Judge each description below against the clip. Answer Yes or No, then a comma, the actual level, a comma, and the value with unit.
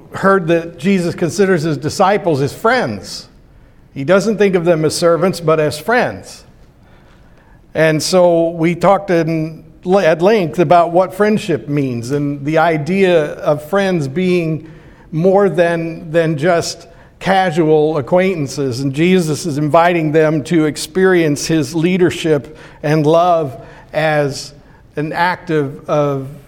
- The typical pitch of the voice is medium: Yes, medium, 165 Hz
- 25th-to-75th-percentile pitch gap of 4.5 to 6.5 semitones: No, average, 2.9 semitones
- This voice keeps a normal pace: No, slow, 130 wpm